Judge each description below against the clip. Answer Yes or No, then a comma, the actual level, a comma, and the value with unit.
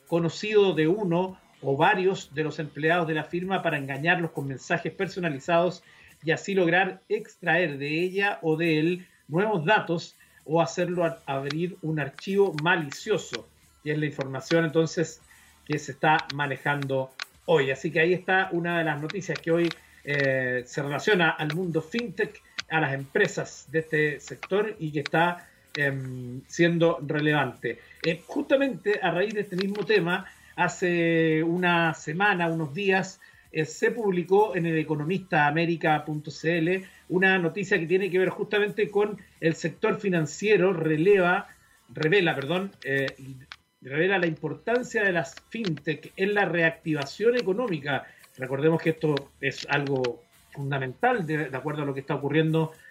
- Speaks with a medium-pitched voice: Yes, medium, 165 Hz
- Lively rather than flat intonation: No, average, 3.7 semitones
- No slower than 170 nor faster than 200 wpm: No, average, 145 wpm